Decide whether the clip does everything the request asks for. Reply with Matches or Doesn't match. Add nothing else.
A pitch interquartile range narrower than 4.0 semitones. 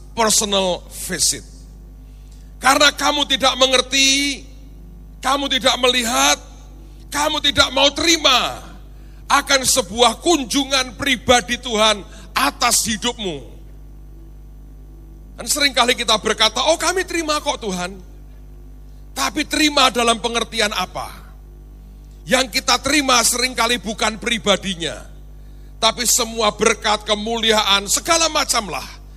Doesn't match